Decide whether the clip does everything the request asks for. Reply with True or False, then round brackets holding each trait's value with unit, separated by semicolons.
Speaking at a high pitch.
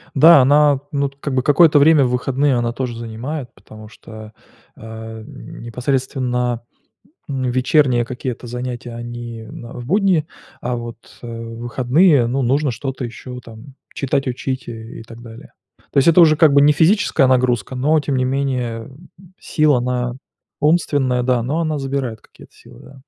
False (125 Hz)